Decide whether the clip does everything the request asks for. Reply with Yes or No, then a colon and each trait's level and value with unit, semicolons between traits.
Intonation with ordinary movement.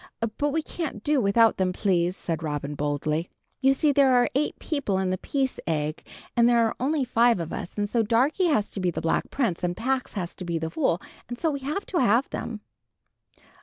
No: wide, 7.4 semitones